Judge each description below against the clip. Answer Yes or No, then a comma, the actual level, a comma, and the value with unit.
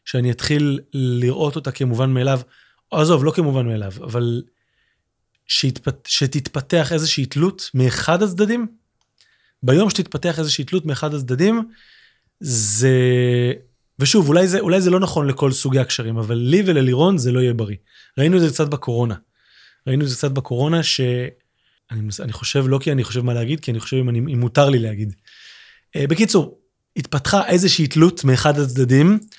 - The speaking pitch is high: No, medium, 140 Hz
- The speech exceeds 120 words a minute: Yes, fast, 150 wpm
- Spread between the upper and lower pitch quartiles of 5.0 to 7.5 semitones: No, average, 4.6 semitones